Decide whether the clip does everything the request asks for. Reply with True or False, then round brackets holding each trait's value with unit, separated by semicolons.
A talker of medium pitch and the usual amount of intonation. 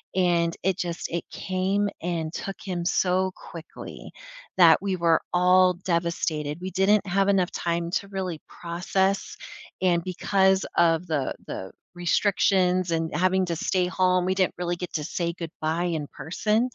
False (180 Hz; 1.9 semitones)